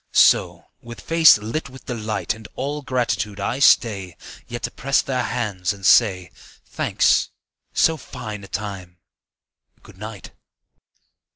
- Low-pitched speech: Yes, low, 110 Hz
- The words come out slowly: Yes, slow, 130 wpm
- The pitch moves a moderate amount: Yes, average, 4.2 semitones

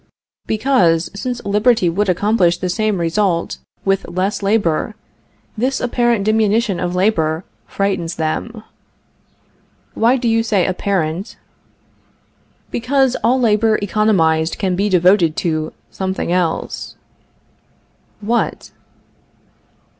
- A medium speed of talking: No, slow, 100 wpm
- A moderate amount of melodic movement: Yes, average, 4.2 semitones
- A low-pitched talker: No, high, 200 Hz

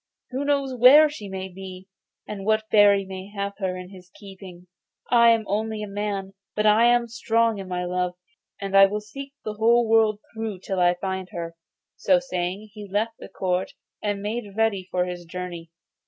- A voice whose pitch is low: No, high, 200 Hz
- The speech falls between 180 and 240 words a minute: Yes, average, 190 wpm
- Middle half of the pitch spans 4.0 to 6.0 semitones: No, average, 3.1 semitones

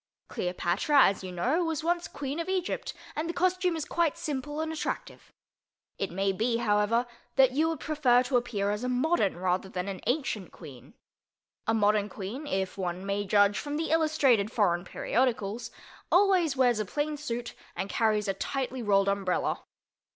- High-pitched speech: Yes, high, 240 Hz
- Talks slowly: No, average, 175 wpm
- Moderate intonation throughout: No, wide, 7.3 semitones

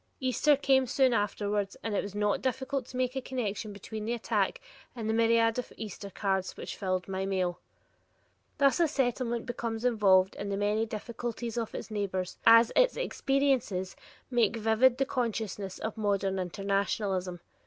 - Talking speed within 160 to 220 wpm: Yes, average, 165 wpm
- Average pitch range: Yes, average, 3.9 semitones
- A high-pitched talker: Yes, high, 220 Hz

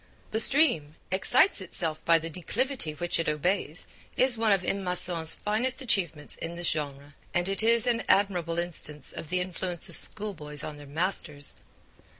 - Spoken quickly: No, average, 165 wpm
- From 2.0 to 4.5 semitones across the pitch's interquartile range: No, average, 5.1 semitones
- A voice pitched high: No, medium, 175 Hz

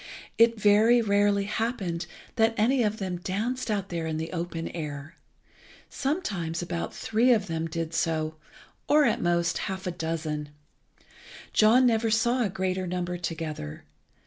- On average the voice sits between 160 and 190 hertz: Yes, medium, 185 Hz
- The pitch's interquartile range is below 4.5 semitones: No, average, 5.2 semitones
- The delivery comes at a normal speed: Yes, average, 150 wpm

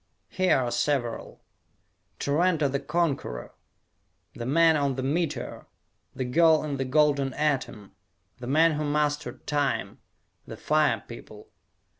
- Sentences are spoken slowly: Yes, slow, 125 wpm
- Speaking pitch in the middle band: Yes, medium, 145 Hz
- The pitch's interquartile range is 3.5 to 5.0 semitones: No, average, 2.8 semitones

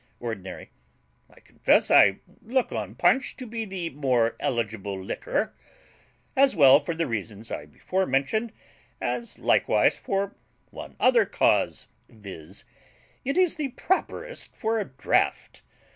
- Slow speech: Yes, slow, 130 wpm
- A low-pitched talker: No, medium, 165 Hz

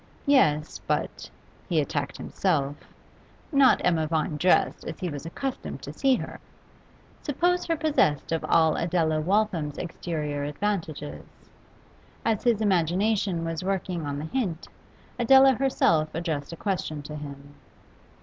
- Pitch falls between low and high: Yes, medium, 165 Hz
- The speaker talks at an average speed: No, slow, 130 wpm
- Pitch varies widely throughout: Yes, wide, 5.9 semitones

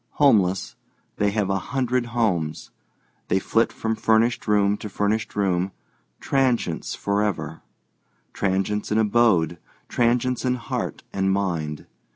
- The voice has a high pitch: No, low, 105 Hz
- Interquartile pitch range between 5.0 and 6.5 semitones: No, average, 3.6 semitones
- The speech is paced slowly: Yes, slow, 115 wpm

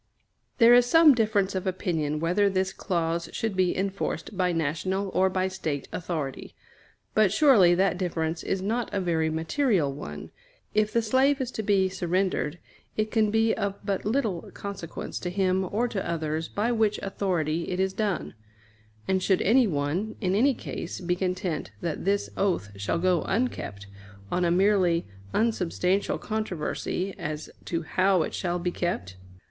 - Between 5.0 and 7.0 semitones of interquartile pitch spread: No, average, 3.7 semitones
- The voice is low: No, medium, 185 Hz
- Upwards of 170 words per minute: No, average, 160 wpm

